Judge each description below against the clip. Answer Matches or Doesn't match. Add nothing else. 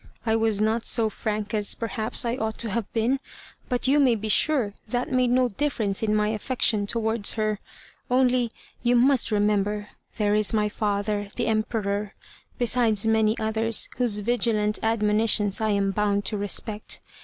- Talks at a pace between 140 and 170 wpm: Matches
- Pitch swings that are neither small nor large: Doesn't match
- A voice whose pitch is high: Matches